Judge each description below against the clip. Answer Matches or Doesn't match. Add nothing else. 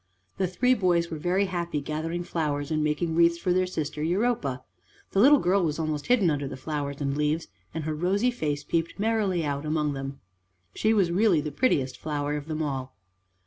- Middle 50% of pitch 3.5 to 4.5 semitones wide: Matches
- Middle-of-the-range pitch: Matches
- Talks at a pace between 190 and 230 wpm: Matches